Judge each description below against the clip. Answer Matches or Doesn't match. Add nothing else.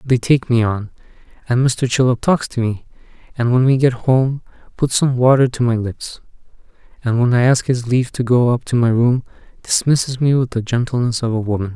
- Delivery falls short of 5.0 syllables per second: Doesn't match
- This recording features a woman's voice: Doesn't match